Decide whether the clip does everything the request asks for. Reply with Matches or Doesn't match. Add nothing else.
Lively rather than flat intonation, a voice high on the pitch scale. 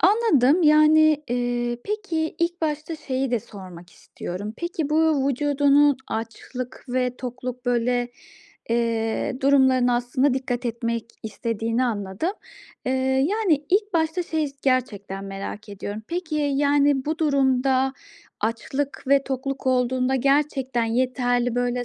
Doesn't match